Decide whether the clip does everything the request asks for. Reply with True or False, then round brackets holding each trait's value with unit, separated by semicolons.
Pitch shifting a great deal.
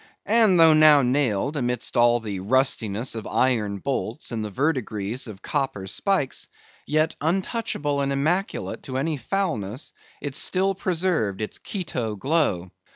True (6.4 semitones)